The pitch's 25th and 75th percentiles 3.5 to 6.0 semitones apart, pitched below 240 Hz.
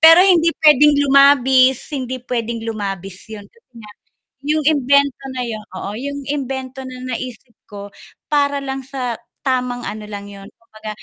No: average, 4.0 semitones; very high, 255 Hz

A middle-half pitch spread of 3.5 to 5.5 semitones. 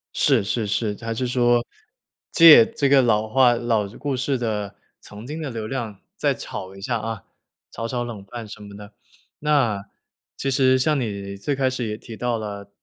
Yes: average, 3.8 semitones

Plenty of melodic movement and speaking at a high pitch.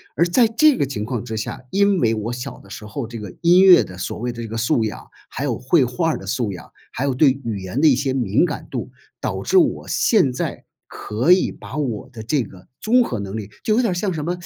No: wide, 7.6 semitones; low, 130 Hz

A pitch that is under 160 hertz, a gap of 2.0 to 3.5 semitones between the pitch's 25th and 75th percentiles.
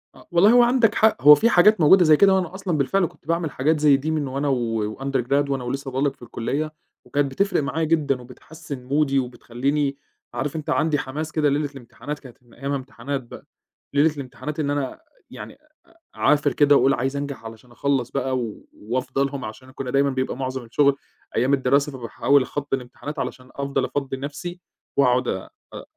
Yes: medium, 140 Hz; narrow, 2.6 semitones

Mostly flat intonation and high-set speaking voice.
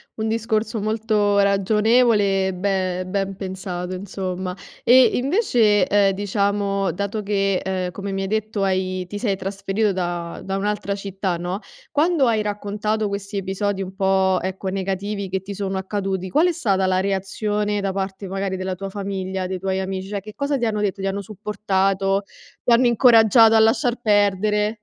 Yes: narrow, 1.8 semitones; high, 200 Hz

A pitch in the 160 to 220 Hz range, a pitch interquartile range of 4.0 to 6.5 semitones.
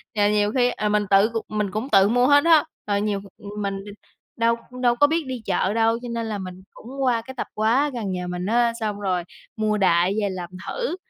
No: high, 215 Hz; average, 3.4 semitones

